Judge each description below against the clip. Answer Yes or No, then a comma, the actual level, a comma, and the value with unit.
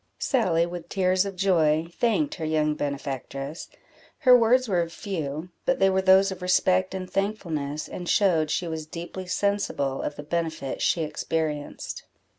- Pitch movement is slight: No, average, 3.9 semitones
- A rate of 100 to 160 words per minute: Yes, average, 155 wpm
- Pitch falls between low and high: Yes, medium, 175 Hz